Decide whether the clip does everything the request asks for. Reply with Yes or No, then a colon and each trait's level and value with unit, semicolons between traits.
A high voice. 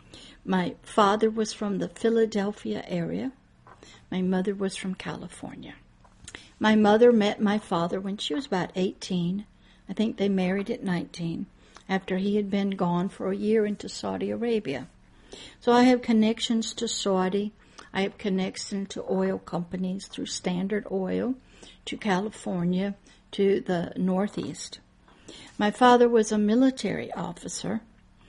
Yes: high, 200 Hz